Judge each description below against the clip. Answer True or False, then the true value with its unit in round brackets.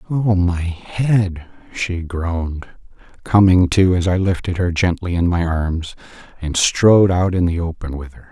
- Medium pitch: False (90 Hz)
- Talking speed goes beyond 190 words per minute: False (165 wpm)